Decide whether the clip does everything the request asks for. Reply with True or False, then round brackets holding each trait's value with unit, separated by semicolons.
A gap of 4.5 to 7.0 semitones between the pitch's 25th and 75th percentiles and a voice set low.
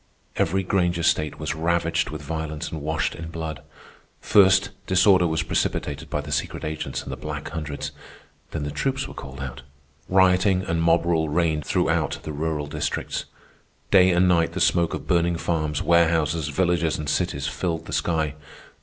False (2.5 semitones; 80 Hz)